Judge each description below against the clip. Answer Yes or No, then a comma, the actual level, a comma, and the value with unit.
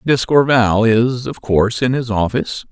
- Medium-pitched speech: No, low, 120 Hz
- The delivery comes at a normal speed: Yes, average, 155 wpm